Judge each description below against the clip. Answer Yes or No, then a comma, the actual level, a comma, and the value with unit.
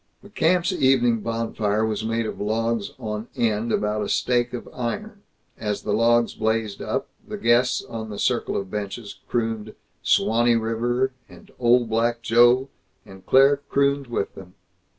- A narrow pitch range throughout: Yes, narrow, 2.1 semitones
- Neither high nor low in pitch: No, low, 115 Hz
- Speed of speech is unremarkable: Yes, average, 155 wpm